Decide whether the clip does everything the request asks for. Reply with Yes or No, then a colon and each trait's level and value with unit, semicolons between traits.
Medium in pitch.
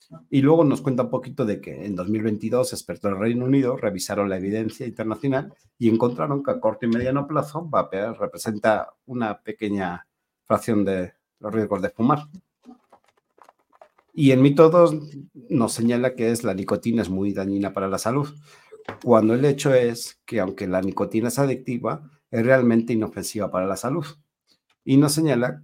No: low, 120 Hz